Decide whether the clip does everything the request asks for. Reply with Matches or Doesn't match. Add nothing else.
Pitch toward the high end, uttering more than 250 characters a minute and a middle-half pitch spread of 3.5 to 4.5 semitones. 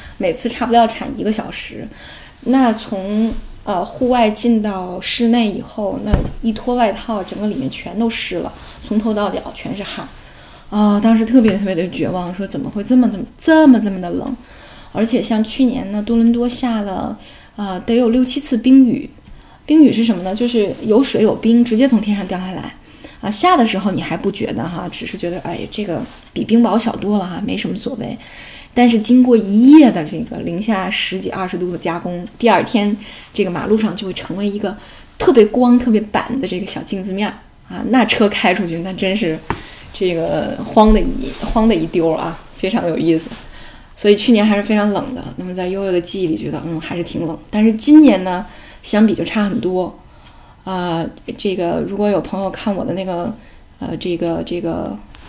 Matches